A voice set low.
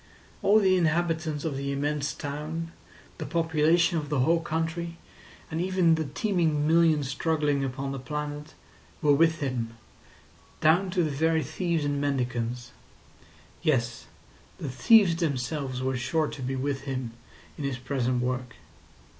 No: medium, 150 Hz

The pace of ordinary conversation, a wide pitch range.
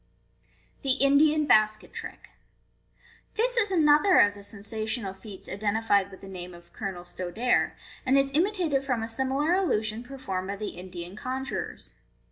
Yes: average, 160 wpm; wide, 6.1 semitones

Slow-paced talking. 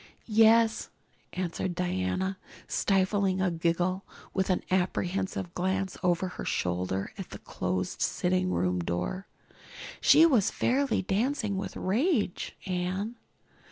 Yes: slow, 115 wpm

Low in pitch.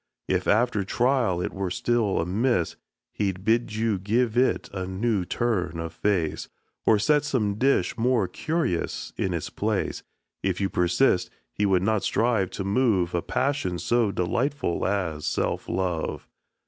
Yes: low, 100 Hz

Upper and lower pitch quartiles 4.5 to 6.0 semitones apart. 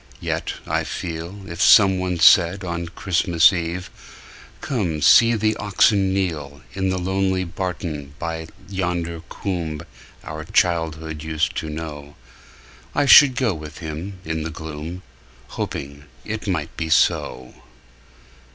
No: average, 3.3 semitones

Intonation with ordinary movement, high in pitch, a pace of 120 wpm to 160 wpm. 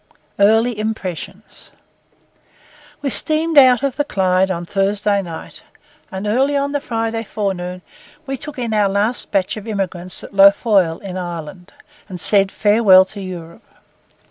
Yes: average, 3.7 semitones; high, 200 Hz; average, 145 wpm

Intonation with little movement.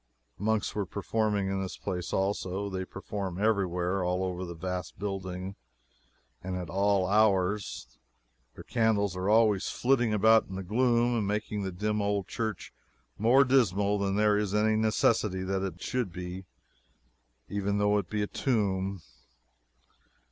Yes: narrow, 2.3 semitones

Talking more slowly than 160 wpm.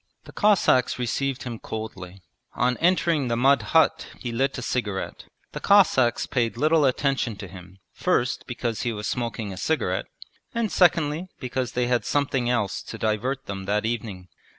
No: average, 165 wpm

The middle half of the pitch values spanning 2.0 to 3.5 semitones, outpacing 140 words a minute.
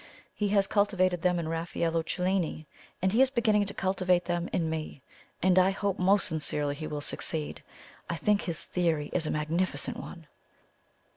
Yes: average, 3.2 semitones; average, 170 wpm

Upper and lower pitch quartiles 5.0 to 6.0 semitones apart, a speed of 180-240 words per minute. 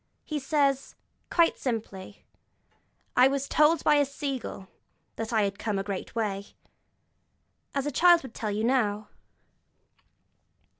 No: wide, 5.4 semitones; slow, 135 wpm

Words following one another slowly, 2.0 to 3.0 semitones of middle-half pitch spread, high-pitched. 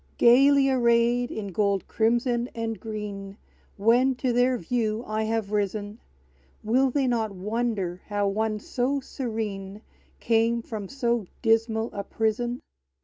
Yes: slow, 130 wpm; narrow, 2.5 semitones; high, 225 Hz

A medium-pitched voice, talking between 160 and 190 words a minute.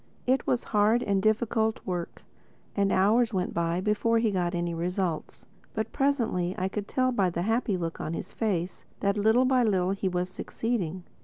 No: high, 200 Hz; average, 180 wpm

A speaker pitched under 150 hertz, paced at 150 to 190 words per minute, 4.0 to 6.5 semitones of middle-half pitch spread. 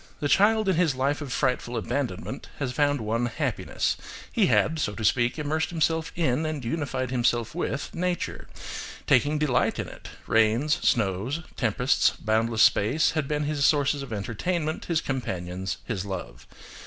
Yes: low, 135 Hz; average, 155 wpm; average, 5.1 semitones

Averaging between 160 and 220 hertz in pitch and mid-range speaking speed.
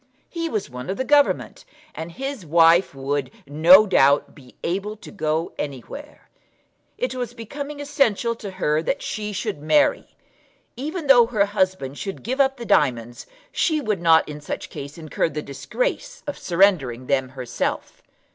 Yes: high, 190 Hz; average, 160 wpm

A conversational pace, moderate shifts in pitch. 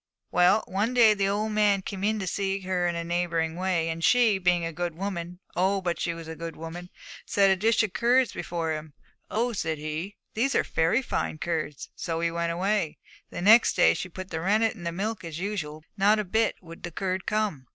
No: fast, 225 wpm; average, 3.8 semitones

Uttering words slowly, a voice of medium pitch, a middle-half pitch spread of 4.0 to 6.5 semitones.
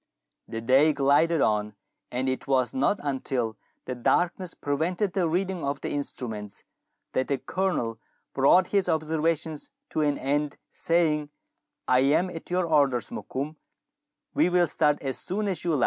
No: average, 165 wpm; medium, 150 Hz; average, 4.5 semitones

